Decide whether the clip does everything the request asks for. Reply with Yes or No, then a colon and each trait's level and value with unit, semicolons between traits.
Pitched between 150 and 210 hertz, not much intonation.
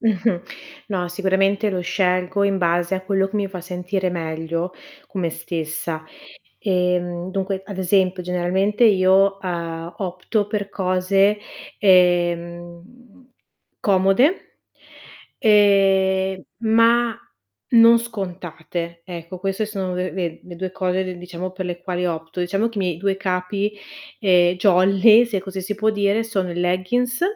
Yes: medium, 185 Hz; narrow, 2.2 semitones